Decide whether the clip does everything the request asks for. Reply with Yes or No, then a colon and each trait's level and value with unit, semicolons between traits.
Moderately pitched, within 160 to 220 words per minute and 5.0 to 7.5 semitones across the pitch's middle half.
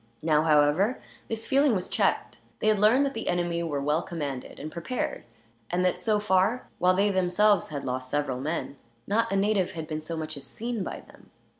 Yes: medium, 180 Hz; average, 200 wpm; wide, 5.4 semitones